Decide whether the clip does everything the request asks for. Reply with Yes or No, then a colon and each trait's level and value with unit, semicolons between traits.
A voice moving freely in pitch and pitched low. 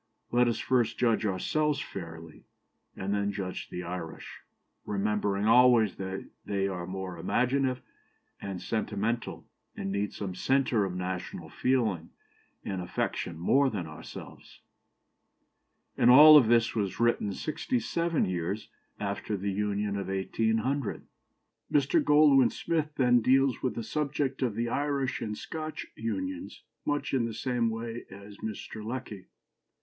No: average, 5.0 semitones; low, 110 Hz